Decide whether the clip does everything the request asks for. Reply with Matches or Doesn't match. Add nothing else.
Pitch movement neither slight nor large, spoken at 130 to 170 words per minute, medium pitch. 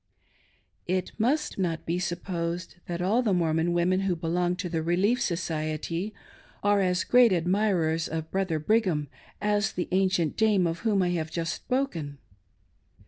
Matches